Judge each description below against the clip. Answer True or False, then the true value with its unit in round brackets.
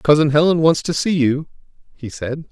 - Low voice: False (150 Hz)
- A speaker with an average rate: True (190 wpm)